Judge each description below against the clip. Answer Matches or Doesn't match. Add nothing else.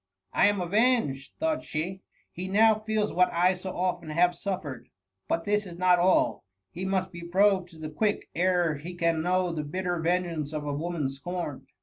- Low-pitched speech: Doesn't match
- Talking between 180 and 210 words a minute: Matches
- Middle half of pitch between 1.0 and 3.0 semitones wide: Matches